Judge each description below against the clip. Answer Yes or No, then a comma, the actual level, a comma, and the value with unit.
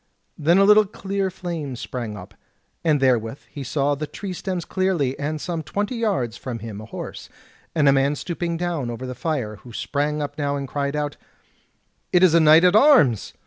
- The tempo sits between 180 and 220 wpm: Yes, average, 195 wpm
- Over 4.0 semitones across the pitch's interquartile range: Yes, average, 5.3 semitones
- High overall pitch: No, medium, 150 Hz